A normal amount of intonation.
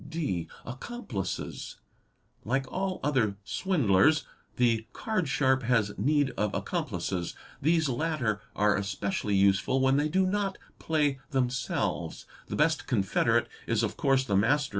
No: wide, 6.4 semitones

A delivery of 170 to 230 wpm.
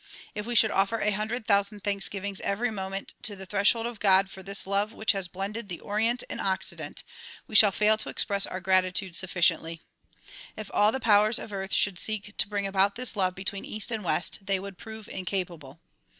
Yes: average, 200 wpm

